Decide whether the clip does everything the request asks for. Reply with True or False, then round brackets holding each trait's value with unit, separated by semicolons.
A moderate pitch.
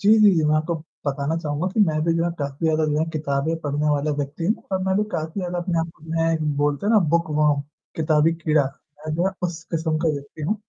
True (160 Hz)